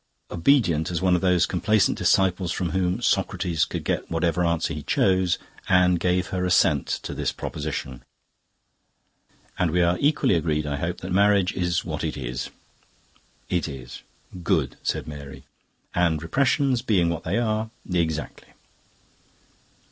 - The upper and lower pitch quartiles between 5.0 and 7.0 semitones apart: No, narrow, 2.6 semitones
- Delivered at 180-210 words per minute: No, average, 145 wpm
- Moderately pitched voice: No, very low, 90 Hz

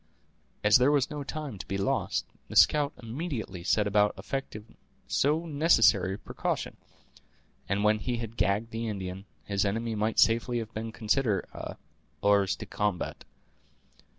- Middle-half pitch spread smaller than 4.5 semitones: Yes, average, 3.8 semitones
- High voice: No, low, 110 Hz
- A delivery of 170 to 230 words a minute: No, average, 150 wpm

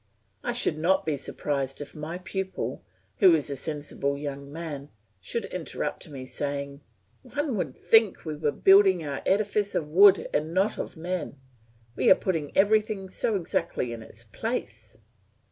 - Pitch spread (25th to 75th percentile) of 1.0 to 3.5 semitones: No, average, 5.0 semitones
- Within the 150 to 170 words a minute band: Yes, average, 160 wpm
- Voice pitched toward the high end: No, medium, 160 Hz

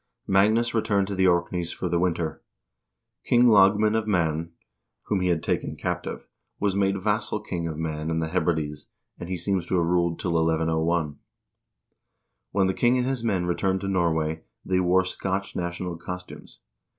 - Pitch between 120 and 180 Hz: No, very low, 90 Hz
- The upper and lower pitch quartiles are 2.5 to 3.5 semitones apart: Yes, average, 2.9 semitones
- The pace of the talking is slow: No, average, 175 wpm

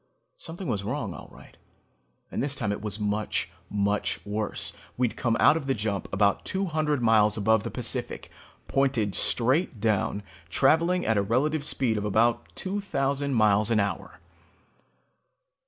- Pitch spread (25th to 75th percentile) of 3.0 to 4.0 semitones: No, average, 5.2 semitones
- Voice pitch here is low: Yes, low, 115 Hz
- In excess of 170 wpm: No, average, 155 wpm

